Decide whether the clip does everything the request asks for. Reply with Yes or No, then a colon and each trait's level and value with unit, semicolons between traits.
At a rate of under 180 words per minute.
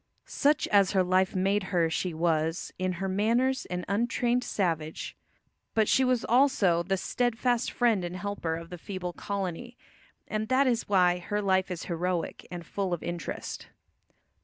Yes: average, 160 wpm